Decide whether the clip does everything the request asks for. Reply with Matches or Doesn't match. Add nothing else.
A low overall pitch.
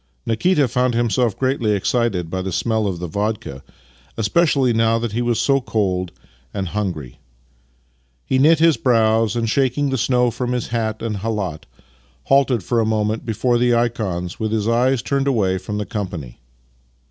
Matches